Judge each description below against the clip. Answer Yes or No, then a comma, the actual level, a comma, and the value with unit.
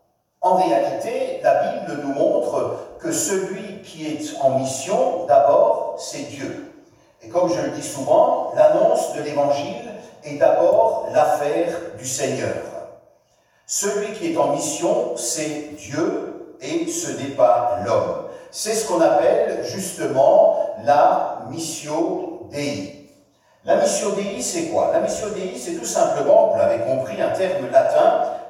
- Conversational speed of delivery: No, slow, 140 wpm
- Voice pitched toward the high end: Yes, very high, 310 Hz